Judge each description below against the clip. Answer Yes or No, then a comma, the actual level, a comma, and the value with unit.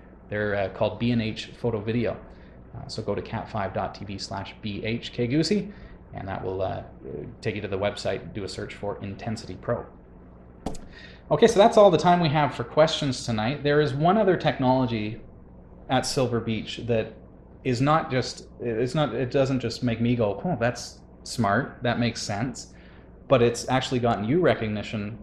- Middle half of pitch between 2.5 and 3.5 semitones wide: No, average, 4.7 semitones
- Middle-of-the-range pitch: No, low, 115 Hz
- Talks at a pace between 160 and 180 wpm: Yes, average, 170 wpm